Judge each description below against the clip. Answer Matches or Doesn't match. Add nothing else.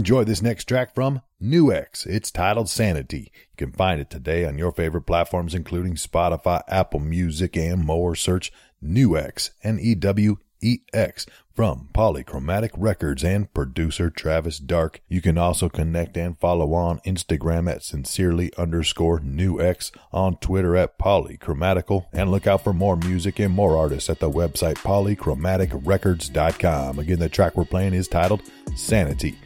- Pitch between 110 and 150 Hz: Doesn't match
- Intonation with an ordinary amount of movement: Matches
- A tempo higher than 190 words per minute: Doesn't match